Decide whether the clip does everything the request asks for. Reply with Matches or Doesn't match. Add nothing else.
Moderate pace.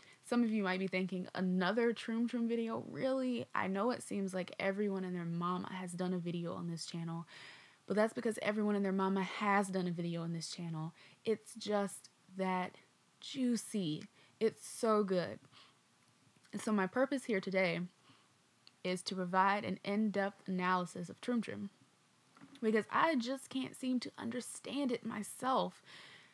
Matches